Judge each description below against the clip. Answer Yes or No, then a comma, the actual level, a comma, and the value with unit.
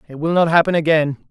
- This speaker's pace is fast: Yes, fast, 230 wpm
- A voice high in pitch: No, medium, 160 Hz